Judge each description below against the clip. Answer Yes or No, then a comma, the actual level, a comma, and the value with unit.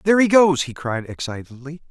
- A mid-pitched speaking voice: Yes, medium, 155 Hz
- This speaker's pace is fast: No, average, 190 wpm